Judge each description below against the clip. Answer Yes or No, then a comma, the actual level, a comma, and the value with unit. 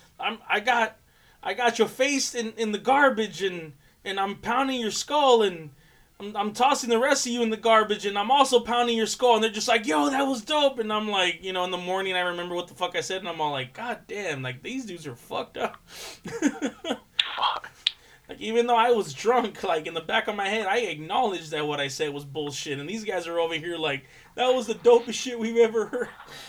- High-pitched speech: Yes, high, 210 Hz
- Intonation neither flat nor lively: No, wide, 5.7 semitones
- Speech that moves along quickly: Yes, fast, 240 wpm